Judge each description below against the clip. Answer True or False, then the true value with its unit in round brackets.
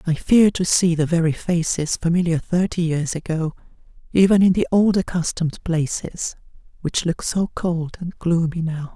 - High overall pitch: False (170 Hz)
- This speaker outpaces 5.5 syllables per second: False (4.7 syllables/s)